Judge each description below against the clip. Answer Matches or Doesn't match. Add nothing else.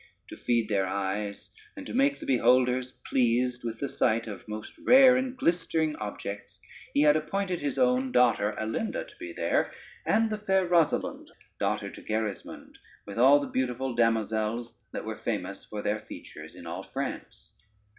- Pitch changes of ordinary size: Doesn't match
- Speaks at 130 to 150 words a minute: Doesn't match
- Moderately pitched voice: Doesn't match